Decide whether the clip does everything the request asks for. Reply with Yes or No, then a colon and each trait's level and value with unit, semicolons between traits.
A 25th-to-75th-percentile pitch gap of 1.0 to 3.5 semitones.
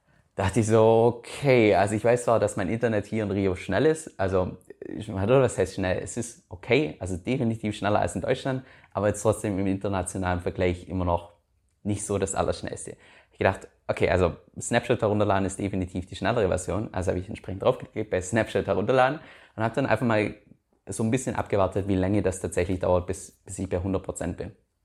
Yes: average, 3.2 semitones